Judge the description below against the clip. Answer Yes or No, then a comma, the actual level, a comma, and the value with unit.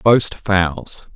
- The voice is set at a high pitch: No, low, 100 Hz